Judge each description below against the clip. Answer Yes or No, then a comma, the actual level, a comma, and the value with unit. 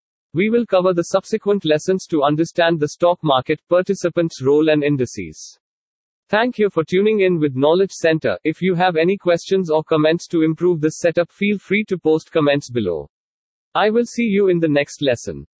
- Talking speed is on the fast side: No, average, 185 wpm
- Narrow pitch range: No, average, 3.8 semitones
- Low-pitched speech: No, medium, 170 Hz